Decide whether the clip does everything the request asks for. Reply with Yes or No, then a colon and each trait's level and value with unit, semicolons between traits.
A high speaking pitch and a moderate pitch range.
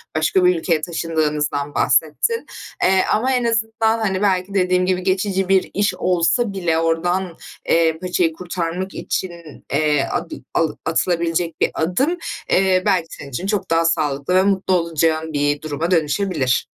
No: medium, 175 Hz; average, 3.0 semitones